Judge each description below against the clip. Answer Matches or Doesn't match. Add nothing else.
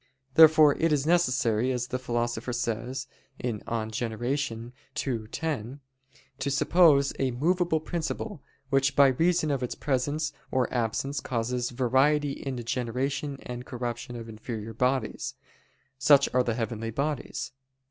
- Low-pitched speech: Matches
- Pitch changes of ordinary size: Matches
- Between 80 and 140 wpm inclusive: Matches